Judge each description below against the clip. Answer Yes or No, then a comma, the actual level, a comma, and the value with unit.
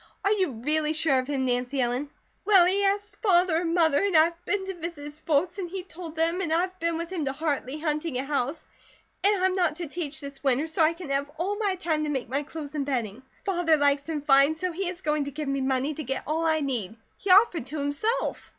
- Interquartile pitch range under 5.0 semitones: Yes, average, 4.0 semitones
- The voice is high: Yes, very high, 315 Hz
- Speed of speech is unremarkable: No, fast, 245 wpm